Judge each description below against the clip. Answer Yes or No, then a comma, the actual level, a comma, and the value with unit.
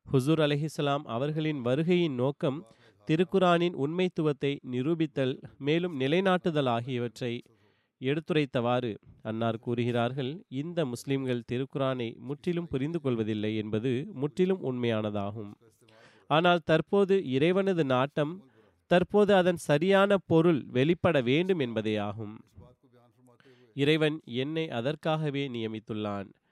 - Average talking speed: Yes, average, 85 wpm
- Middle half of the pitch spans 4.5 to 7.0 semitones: Yes, average, 5.1 semitones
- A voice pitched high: No, low, 135 Hz